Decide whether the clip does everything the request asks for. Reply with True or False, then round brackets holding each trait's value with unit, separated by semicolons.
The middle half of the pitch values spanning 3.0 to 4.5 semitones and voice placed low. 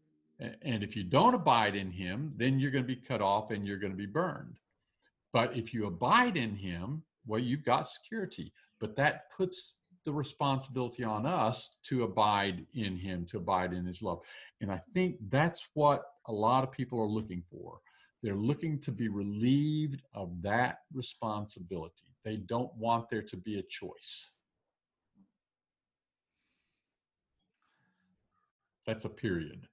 False (5.0 semitones; 115 Hz)